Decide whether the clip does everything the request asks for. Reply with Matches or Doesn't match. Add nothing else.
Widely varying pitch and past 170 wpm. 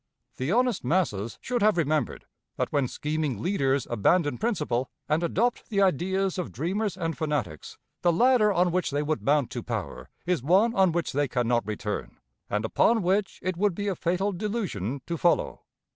Matches